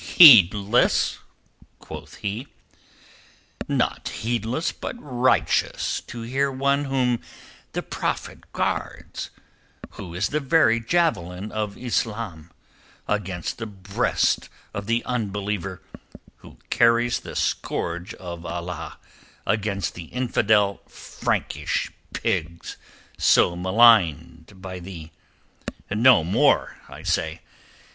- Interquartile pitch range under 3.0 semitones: No, average, 4.7 semitones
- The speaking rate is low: Yes, slow, 100 wpm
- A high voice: No, low, 105 Hz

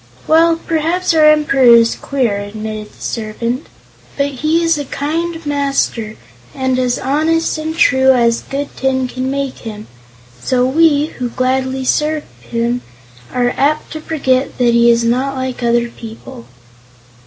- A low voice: No, very high, 265 Hz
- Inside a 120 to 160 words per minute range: Yes, average, 150 wpm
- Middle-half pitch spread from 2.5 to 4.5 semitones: Yes, average, 4.2 semitones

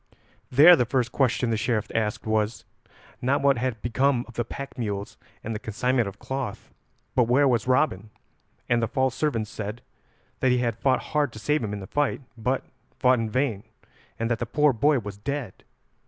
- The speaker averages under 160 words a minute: No, average, 195 wpm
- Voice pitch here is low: Yes, low, 120 Hz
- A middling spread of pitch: Yes, average, 3.4 semitones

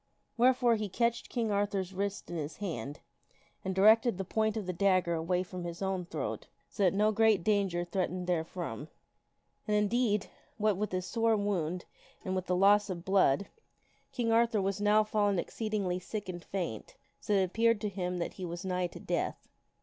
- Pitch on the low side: No, high, 195 Hz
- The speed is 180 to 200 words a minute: Yes, average, 195 wpm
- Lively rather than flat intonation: No, average, 2.9 semitones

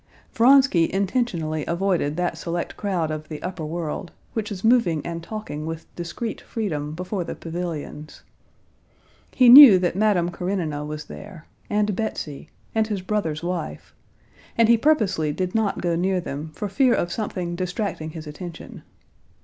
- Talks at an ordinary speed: Yes, average, 150 wpm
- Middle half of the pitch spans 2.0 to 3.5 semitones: No, average, 4.5 semitones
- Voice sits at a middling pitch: Yes, medium, 180 Hz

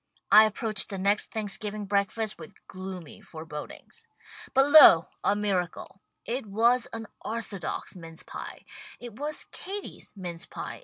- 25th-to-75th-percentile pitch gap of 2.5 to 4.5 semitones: Yes, average, 3.5 semitones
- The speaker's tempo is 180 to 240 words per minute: No, average, 140 wpm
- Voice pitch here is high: Yes, high, 205 Hz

